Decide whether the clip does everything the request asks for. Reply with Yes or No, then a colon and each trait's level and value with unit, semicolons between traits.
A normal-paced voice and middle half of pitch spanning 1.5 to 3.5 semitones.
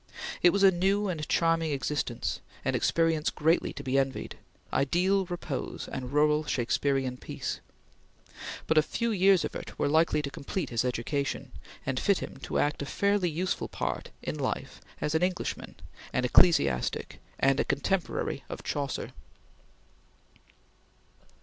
No: average, 145 wpm; average, 4.6 semitones